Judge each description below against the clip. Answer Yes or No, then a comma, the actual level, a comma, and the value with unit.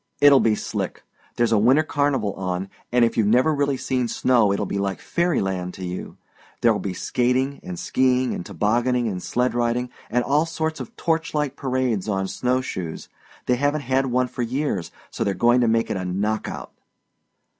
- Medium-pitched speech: No, low, 120 Hz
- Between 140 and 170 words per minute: No, average, 190 wpm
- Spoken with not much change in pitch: No, average, 4.5 semitones